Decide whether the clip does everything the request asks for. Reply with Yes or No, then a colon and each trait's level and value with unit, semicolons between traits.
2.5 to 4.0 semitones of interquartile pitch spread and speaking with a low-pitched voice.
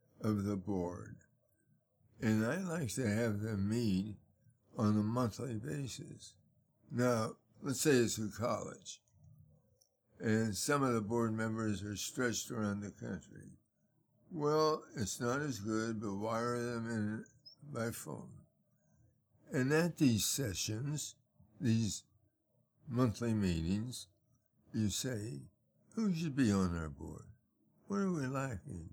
Yes: average, 3.6 semitones; low, 115 Hz